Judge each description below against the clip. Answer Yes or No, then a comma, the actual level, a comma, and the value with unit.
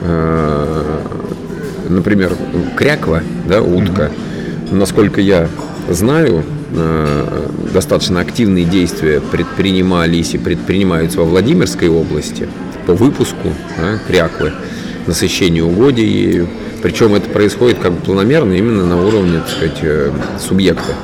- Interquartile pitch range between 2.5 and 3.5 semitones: Yes, average, 2.8 semitones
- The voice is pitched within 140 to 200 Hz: No, very low, 85 Hz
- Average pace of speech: No, slow, 95 wpm